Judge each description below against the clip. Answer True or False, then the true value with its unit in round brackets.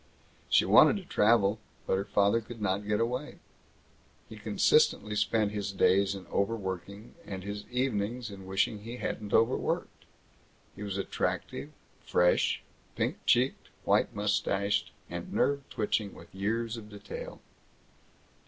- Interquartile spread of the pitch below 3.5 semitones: True (2.5 semitones)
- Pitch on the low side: True (105 Hz)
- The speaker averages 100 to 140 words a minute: True (135 wpm)